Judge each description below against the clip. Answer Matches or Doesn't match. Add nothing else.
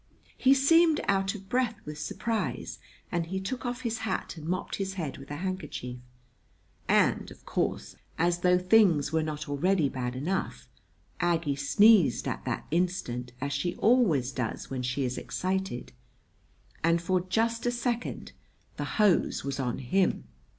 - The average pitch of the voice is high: Doesn't match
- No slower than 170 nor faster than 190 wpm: Doesn't match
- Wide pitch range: Matches